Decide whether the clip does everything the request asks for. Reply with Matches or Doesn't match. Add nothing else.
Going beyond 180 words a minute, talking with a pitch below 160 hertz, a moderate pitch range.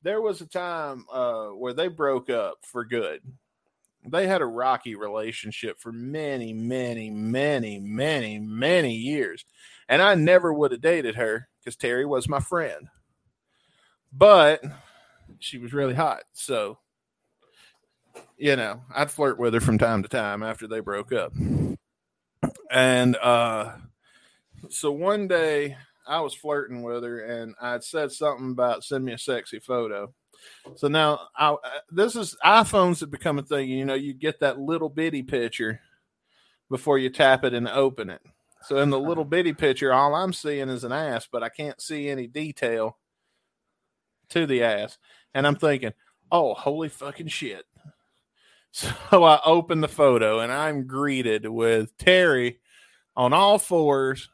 Doesn't match